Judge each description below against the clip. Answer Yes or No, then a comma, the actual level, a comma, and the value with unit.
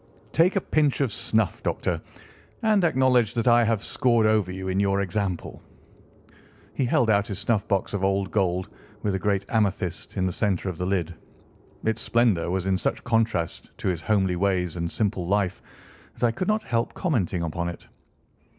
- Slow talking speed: No, average, 180 wpm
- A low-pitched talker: Yes, low, 100 Hz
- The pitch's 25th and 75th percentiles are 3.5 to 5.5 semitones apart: Yes, average, 3.9 semitones